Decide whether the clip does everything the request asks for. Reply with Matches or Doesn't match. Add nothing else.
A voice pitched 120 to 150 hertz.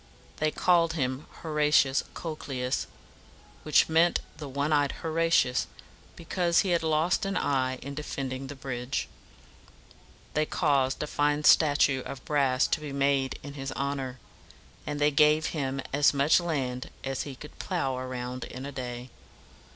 Matches